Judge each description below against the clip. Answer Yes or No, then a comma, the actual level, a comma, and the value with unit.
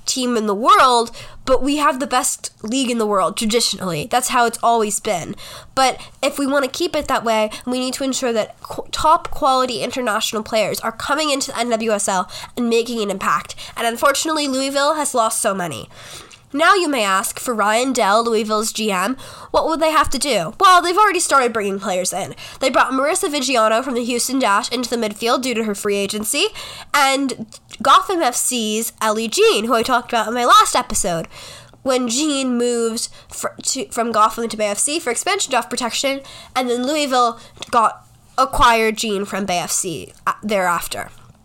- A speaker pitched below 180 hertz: No, high, 245 Hz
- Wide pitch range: No, average, 4.0 semitones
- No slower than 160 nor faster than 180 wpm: No, average, 190 wpm